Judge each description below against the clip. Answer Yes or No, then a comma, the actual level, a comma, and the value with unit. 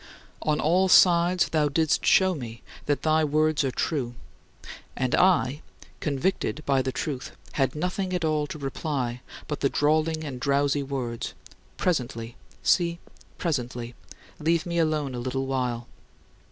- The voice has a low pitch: No, medium, 145 Hz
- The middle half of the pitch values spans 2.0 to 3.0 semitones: No, average, 3.6 semitones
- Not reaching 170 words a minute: Yes, average, 145 wpm